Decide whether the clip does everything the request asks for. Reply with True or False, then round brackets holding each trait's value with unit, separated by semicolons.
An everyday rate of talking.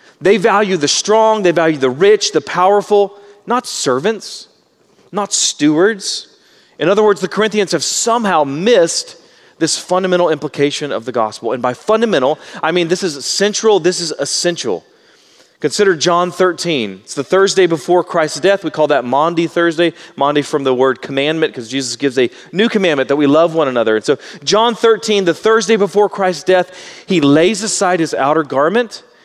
True (170 wpm)